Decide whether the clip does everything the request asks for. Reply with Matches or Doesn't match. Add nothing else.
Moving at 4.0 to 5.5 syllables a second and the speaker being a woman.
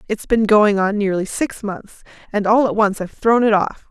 Matches